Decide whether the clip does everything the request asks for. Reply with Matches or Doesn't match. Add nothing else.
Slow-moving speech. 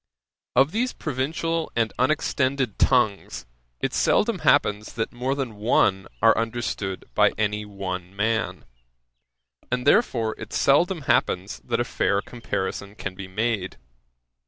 Matches